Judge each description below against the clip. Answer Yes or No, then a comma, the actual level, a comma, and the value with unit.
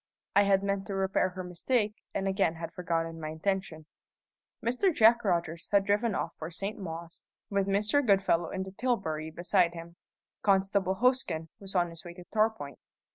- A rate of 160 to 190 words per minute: Yes, average, 175 wpm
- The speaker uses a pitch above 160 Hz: Yes, high, 190 Hz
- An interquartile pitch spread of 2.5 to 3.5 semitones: Yes, average, 3.1 semitones